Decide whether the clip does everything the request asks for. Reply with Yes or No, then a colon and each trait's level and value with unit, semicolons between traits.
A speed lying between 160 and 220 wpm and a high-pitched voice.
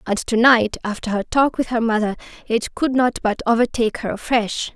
Yes: average, 200 wpm; high, 230 Hz